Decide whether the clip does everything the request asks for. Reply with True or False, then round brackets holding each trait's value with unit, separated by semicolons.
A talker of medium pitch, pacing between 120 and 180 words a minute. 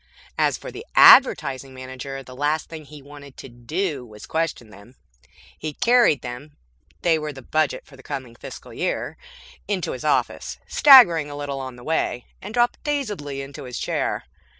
True (145 Hz; 175 wpm)